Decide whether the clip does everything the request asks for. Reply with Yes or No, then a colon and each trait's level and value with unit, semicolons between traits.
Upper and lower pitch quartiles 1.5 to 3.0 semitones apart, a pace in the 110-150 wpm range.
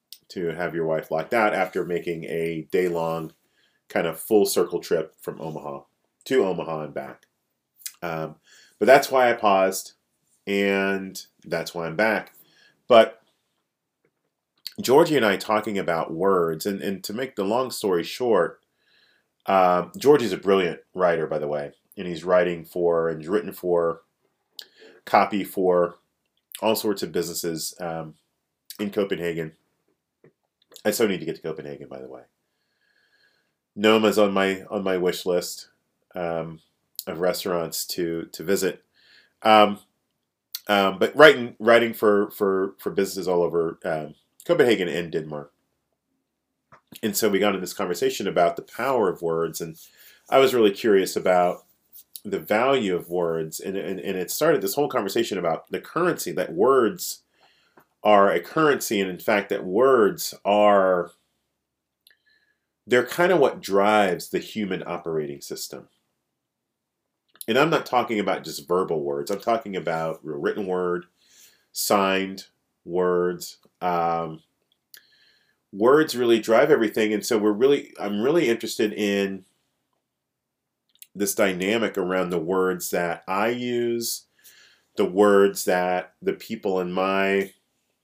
No: average, 3.7 semitones; average, 140 wpm